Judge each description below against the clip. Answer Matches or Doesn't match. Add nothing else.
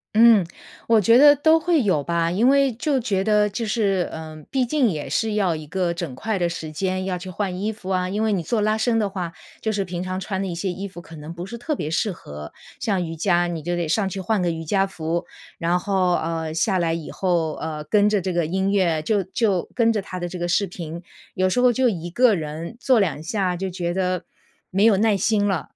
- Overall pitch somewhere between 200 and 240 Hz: Doesn't match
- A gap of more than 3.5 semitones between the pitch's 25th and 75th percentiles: Matches